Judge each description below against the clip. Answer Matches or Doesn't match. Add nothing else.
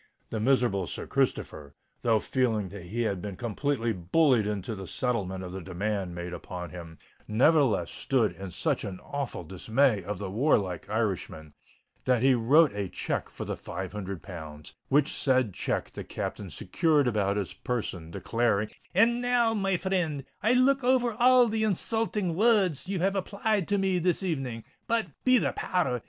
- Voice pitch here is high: Doesn't match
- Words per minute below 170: Doesn't match